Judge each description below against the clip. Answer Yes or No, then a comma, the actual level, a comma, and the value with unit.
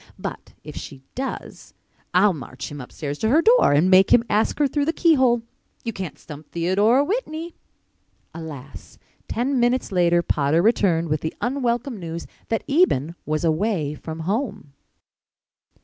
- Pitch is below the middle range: No, high, 195 Hz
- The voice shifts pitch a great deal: Yes, wide, 8.0 semitones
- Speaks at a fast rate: No, average, 150 wpm